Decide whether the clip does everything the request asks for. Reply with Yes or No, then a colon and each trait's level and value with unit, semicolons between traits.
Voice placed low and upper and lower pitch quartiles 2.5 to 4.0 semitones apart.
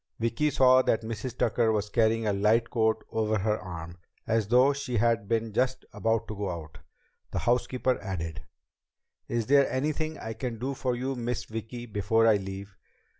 Yes: low, 115 Hz; average, 3.1 semitones